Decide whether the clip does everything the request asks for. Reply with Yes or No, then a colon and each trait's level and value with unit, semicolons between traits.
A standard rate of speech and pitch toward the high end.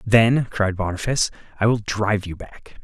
No: average, 170 wpm; low, 105 Hz